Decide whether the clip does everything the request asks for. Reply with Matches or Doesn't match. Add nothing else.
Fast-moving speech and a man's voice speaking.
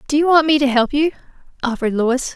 Doesn't match